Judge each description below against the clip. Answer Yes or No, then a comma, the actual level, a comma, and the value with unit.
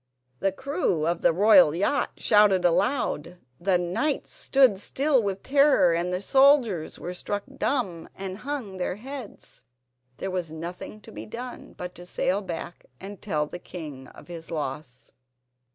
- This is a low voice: No, high, 190 Hz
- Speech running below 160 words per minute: Yes, average, 150 wpm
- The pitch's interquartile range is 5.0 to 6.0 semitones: Yes, average, 5.3 semitones